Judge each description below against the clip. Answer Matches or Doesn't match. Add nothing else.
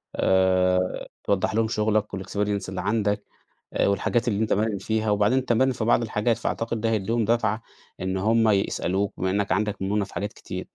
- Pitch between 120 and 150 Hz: Doesn't match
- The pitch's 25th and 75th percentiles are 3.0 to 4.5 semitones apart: Doesn't match